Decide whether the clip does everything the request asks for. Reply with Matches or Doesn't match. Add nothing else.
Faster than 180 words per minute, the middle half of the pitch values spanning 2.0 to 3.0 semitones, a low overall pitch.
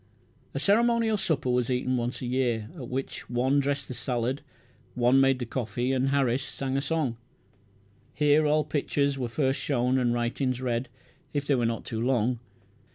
Doesn't match